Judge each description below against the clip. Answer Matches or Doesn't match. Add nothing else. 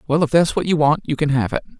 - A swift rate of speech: Matches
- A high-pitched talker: Doesn't match